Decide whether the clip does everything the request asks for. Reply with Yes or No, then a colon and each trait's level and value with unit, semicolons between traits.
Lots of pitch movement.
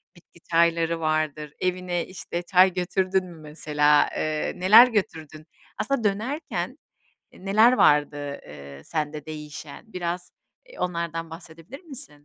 No: average, 3.6 semitones